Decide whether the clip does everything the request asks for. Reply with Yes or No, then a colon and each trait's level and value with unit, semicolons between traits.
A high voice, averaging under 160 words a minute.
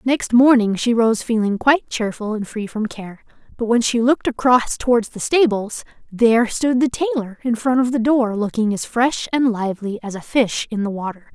No: high, 230 Hz; fast, 205 wpm